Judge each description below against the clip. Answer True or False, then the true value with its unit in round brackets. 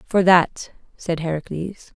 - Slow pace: True (120 wpm)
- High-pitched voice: False (170 Hz)